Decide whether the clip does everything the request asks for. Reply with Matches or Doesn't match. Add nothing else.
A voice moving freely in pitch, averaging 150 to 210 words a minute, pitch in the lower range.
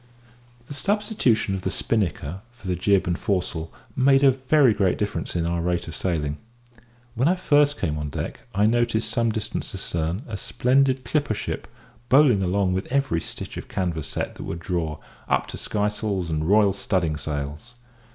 Matches